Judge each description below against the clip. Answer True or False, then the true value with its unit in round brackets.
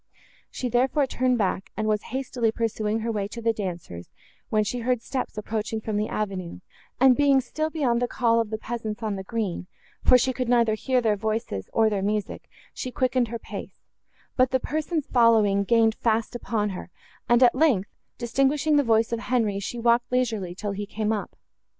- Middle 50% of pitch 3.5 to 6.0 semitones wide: False (2.9 semitones)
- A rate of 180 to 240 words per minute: True (195 wpm)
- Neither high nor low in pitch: False (230 Hz)